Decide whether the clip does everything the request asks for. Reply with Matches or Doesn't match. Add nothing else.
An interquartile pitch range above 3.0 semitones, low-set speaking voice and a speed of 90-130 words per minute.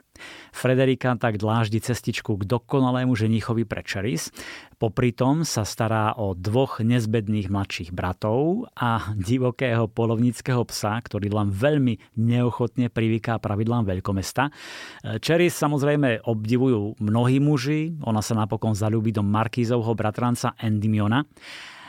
Doesn't match